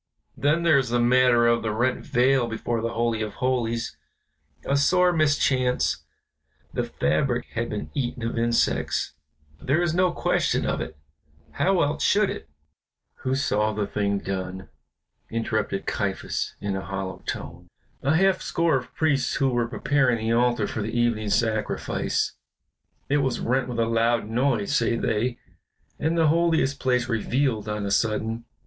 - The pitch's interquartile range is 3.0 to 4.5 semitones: Yes, average, 3.8 semitones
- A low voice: Yes, low, 120 Hz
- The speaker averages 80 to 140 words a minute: No, average, 160 wpm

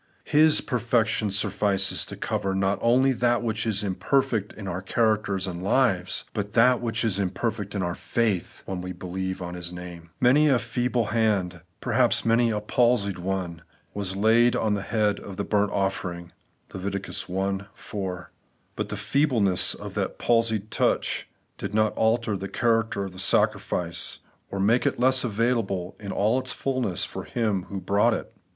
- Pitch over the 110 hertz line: No, low, 105 Hz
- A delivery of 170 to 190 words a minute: Yes, average, 175 wpm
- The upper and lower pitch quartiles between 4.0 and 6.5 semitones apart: No, average, 3.5 semitones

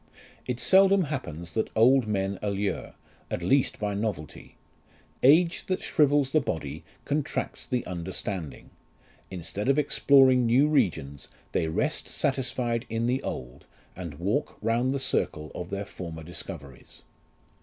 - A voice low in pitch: Yes, low, 110 Hz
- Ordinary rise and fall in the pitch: No, wide, 7.6 semitones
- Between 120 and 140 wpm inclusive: Yes, slow, 135 wpm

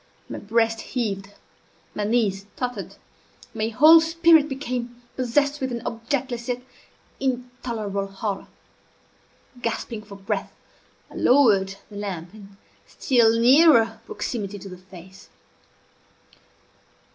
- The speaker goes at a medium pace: No, slow, 110 wpm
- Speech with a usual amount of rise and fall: Yes, average, 4.0 semitones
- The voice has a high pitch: Yes, high, 230 Hz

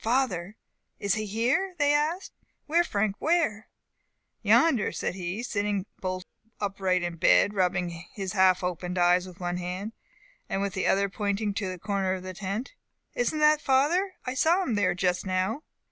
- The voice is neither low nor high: No, high, 200 Hz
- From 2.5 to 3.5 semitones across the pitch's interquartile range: No, wide, 5.4 semitones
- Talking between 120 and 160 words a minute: No, average, 170 wpm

